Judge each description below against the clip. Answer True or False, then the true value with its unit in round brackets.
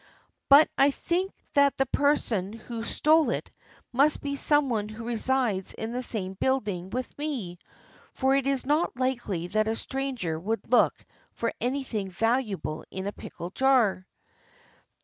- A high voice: True (240 Hz)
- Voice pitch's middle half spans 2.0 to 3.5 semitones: False (4.8 semitones)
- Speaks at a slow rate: False (150 wpm)